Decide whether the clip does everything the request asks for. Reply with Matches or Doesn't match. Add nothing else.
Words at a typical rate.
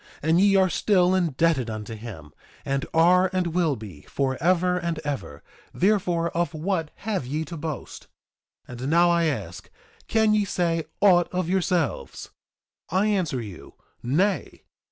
Matches